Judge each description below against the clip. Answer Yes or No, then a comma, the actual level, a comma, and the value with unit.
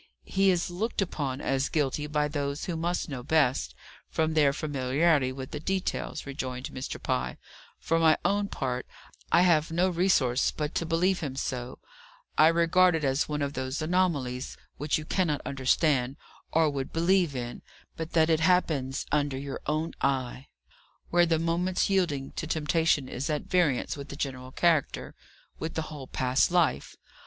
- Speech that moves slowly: No, average, 165 wpm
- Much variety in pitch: No, average, 3.8 semitones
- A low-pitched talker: No, medium, 150 Hz